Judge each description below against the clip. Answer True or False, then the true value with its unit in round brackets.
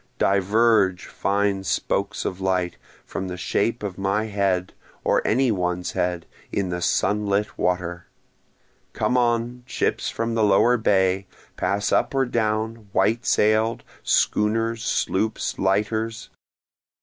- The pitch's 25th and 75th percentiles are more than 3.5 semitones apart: False (3.0 semitones)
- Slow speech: True (125 wpm)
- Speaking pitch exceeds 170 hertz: False (100 Hz)